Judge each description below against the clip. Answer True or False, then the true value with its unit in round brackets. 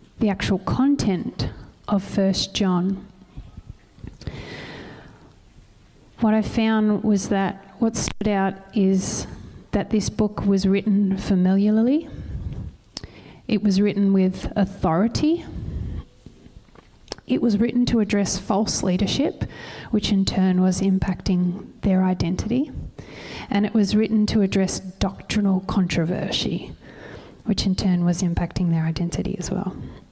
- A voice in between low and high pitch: False (195 Hz)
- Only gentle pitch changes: True (2.2 semitones)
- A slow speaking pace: True (115 wpm)